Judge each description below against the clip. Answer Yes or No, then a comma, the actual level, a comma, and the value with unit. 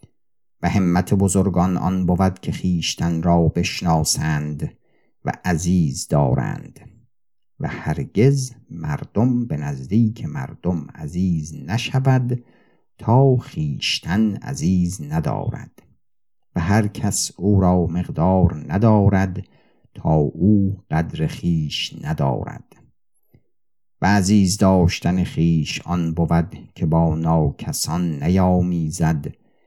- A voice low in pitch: Yes, very low, 95 Hz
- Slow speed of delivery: Yes, slow, 95 wpm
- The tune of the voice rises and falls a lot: No, average, 4.9 semitones